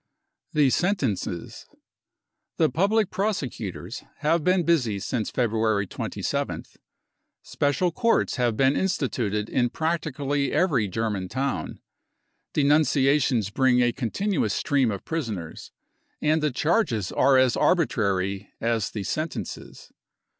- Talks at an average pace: No, slow, 110 wpm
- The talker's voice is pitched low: Yes, low, 130 Hz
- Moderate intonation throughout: No, wide, 6.2 semitones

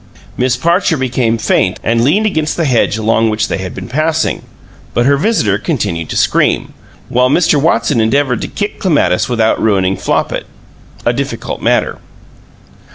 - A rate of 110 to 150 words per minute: No, average, 160 wpm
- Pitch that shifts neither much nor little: No, wide, 5.9 semitones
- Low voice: Yes, low, 125 Hz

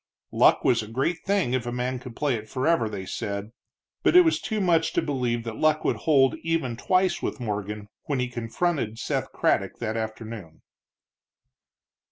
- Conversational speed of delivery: Yes, average, 180 wpm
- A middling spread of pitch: No, wide, 5.9 semitones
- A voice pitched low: Yes, low, 125 Hz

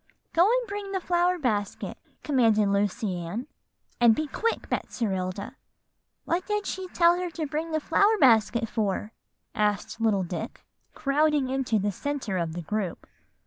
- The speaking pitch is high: Yes, very high, 250 Hz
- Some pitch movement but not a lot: No, wide, 8.6 semitones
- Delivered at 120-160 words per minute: Yes, average, 150 wpm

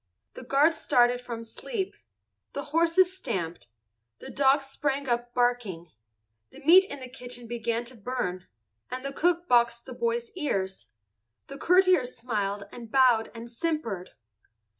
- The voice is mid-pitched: No, very high, 250 Hz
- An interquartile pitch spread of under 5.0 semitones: Yes, average, 4.6 semitones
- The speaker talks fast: No, average, 140 wpm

